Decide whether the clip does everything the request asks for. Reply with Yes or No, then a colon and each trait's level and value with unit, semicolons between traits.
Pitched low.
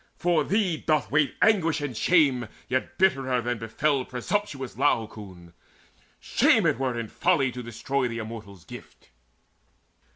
Yes: low, 130 Hz